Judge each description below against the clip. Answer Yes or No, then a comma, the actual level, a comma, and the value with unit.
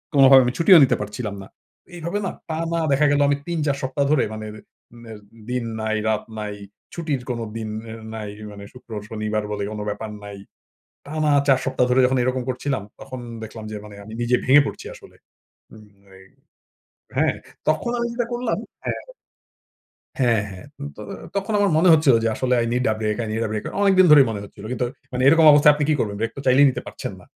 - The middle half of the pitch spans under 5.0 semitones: No, wide, 5.5 semitones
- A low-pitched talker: Yes, low, 125 Hz